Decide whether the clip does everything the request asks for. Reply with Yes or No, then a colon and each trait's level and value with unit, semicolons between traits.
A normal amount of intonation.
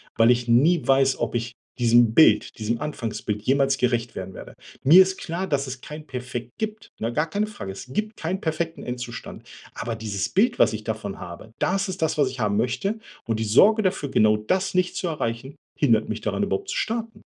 No: wide, 8.0 semitones